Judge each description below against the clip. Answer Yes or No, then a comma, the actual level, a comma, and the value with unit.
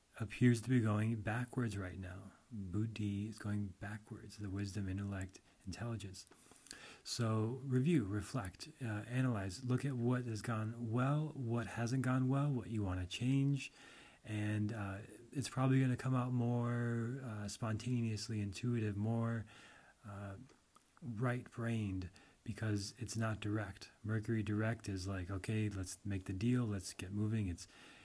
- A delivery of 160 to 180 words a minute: No, average, 145 wpm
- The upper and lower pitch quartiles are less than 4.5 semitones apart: Yes, average, 3.2 semitones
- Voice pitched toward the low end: Yes, low, 110 Hz